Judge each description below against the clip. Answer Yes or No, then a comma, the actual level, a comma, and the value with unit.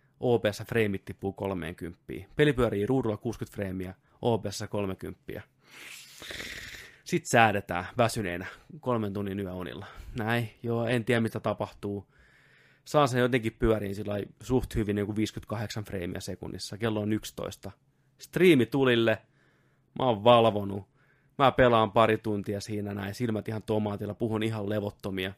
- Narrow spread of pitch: No, average, 3.1 semitones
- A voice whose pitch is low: Yes, low, 110 Hz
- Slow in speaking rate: No, average, 130 wpm